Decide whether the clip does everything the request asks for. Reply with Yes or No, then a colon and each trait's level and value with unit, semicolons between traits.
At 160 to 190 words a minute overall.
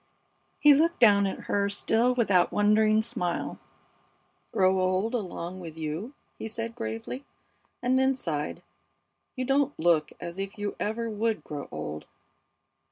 No: average, 150 wpm